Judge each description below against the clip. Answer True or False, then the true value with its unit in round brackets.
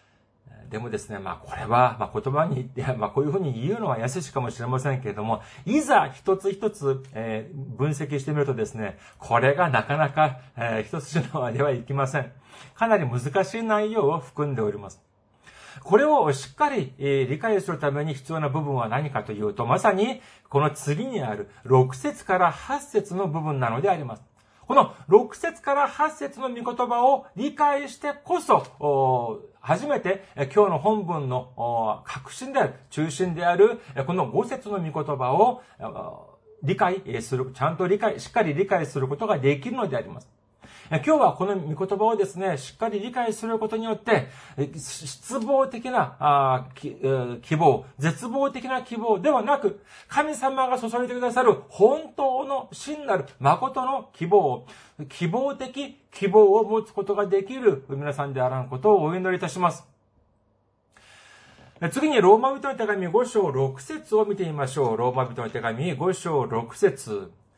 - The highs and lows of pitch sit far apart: True (8.9 semitones)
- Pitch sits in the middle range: True (170 Hz)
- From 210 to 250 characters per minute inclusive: False (310 characters per minute)